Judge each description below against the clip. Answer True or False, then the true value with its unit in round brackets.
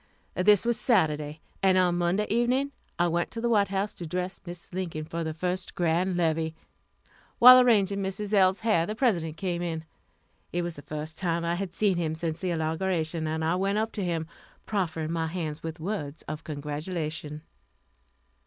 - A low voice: False (175 Hz)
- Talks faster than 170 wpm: True (180 wpm)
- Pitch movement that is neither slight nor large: True (3.4 semitones)